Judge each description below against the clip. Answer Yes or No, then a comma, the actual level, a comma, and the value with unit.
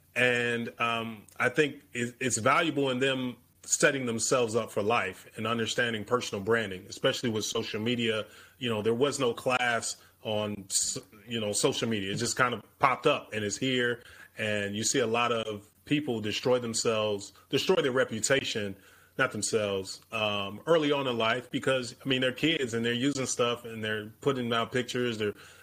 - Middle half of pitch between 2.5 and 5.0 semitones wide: Yes, average, 3.0 semitones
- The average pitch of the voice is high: No, low, 115 Hz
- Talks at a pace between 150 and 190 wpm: Yes, average, 175 wpm